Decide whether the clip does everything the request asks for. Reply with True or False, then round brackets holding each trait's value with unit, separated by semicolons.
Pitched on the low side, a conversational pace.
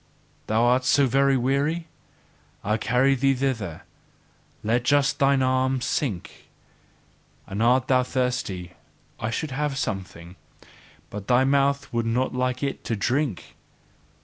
False (130 Hz; 130 wpm)